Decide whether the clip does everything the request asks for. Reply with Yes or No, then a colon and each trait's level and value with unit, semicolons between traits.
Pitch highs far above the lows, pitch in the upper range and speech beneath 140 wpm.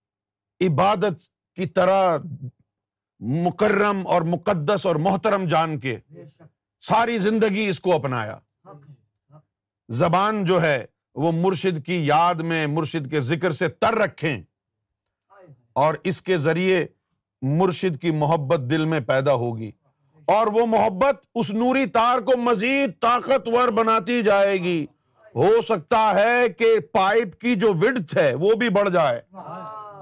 No: wide, 6.4 semitones; medium, 180 Hz; average, 130 wpm